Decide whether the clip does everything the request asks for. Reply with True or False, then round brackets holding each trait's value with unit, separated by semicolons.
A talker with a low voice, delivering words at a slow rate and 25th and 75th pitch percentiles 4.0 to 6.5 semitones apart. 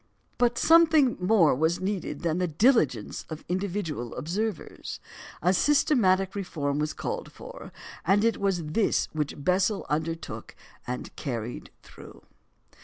False (185 Hz; 125 wpm; 5.1 semitones)